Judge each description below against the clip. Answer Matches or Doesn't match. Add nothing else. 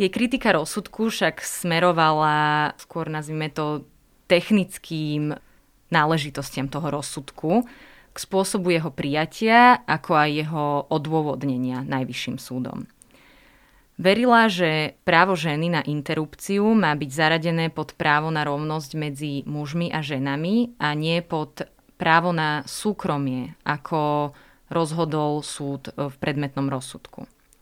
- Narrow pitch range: Doesn't match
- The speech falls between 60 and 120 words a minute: Matches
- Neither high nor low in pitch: Matches